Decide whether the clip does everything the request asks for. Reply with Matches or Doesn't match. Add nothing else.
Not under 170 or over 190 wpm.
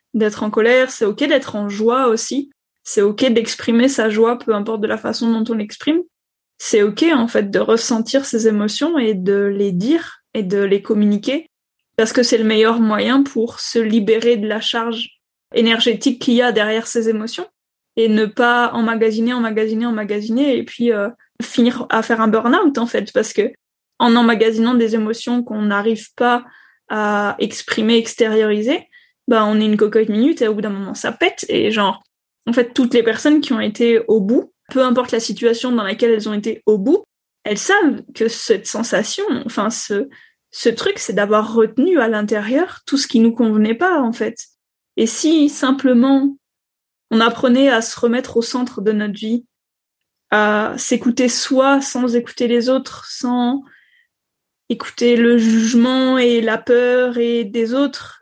Matches